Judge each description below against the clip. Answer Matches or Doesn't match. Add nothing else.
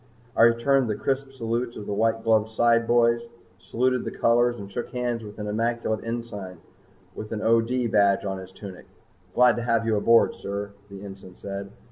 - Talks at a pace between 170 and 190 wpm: Matches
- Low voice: Matches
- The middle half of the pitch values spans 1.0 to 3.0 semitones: Matches